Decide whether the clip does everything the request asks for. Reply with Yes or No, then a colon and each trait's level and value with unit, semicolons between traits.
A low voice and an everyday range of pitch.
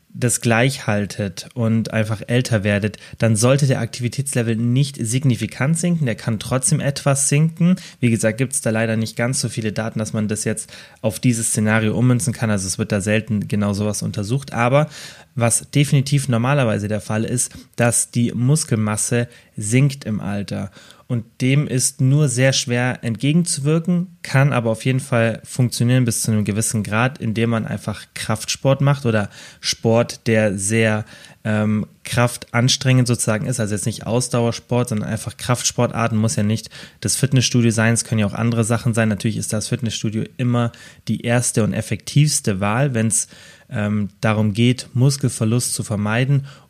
Yes: low, 115 Hz; average, 3.0 semitones